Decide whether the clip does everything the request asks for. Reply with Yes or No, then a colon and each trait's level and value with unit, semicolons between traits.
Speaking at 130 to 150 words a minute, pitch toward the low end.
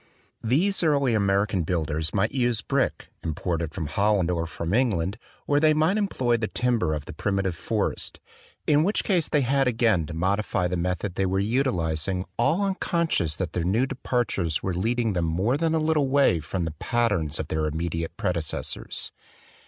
No: average, 175 wpm; low, 100 Hz